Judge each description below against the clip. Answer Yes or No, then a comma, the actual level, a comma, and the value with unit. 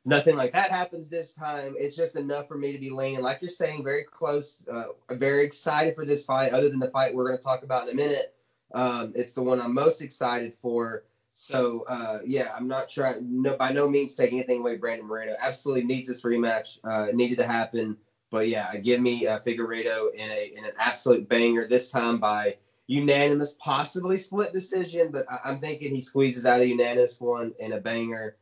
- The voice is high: No, low, 130 Hz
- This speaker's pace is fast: Yes, fast, 215 wpm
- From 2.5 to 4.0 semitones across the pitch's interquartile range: Yes, average, 3.3 semitones